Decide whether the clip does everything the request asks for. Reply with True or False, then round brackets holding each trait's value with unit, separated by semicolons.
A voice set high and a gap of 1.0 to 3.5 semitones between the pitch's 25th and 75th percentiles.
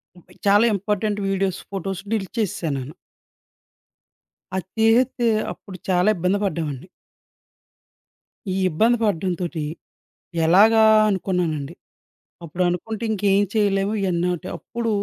True (195 Hz; 3.1 semitones)